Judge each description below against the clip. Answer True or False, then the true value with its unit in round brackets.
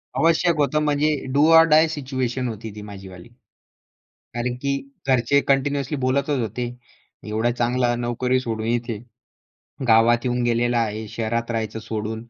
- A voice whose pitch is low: True (120 Hz)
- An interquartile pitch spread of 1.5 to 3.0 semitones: False (3.4 semitones)